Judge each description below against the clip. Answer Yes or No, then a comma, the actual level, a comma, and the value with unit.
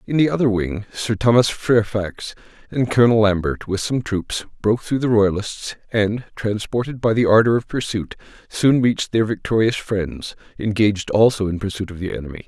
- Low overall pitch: Yes, low, 110 Hz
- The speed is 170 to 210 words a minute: Yes, average, 175 wpm